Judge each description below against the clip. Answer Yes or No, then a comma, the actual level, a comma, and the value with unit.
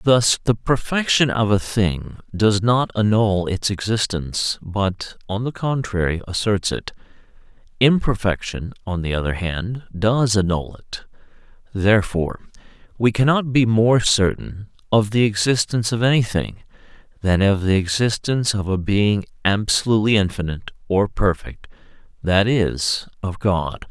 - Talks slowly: Yes, slow, 125 wpm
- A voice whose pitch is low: Yes, low, 105 Hz